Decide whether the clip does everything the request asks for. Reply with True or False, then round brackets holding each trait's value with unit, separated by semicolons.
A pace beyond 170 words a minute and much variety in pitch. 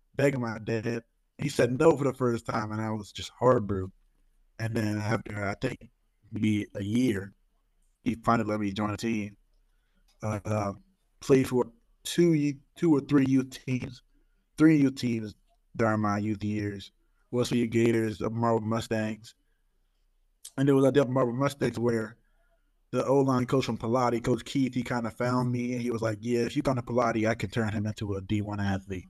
False (185 wpm; 2.9 semitones)